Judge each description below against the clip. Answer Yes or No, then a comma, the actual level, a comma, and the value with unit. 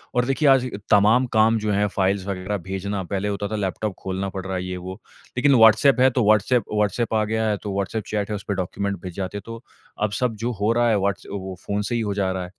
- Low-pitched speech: Yes, low, 105 Hz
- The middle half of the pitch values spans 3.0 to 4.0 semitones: No, narrow, 2.5 semitones